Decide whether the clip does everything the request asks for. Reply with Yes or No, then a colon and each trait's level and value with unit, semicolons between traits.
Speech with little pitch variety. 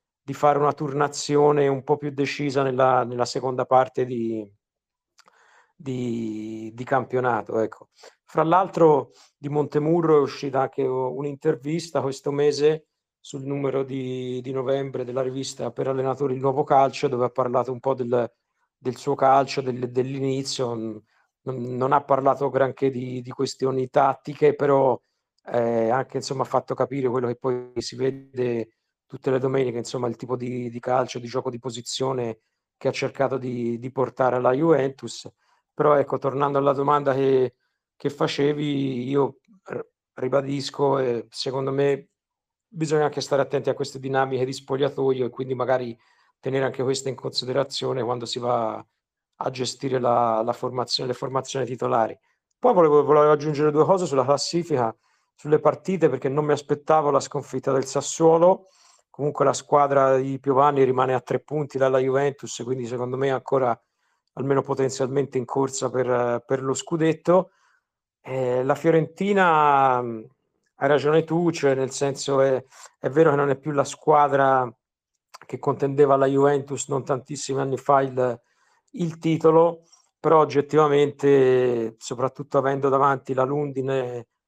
Yes: narrow, 2.0 semitones